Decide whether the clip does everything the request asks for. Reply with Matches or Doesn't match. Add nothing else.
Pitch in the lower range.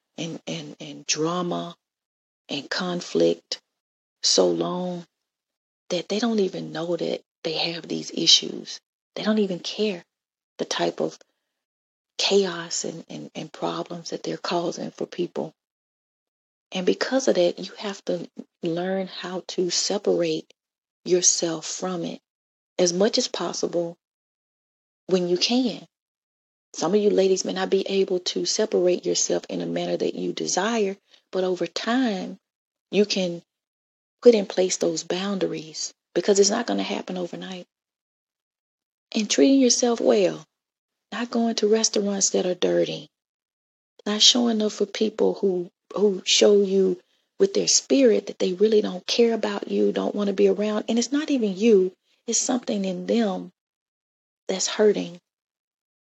Doesn't match